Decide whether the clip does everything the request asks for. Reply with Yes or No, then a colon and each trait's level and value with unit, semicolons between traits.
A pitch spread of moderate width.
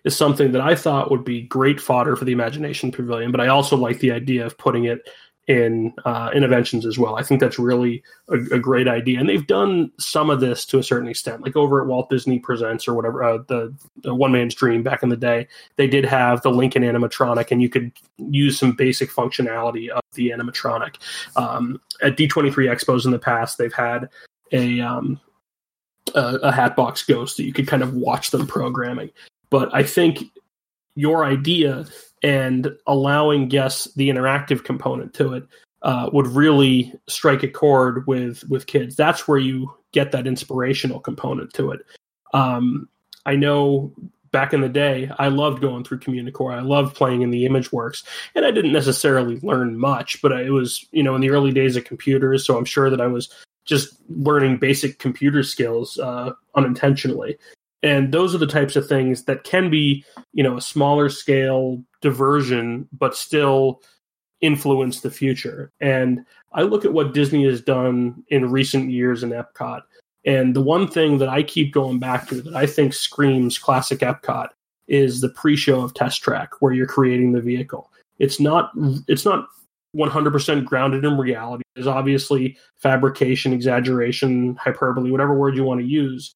No: narrow, 2.1 semitones